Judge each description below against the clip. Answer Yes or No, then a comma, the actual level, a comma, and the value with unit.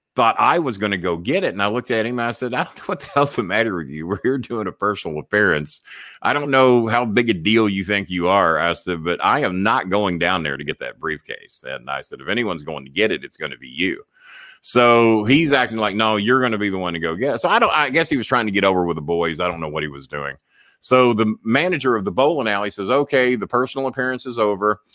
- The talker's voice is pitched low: Yes, low, 110 Hz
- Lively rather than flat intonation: Yes, wide, 6.1 semitones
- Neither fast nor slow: No, fast, 290 wpm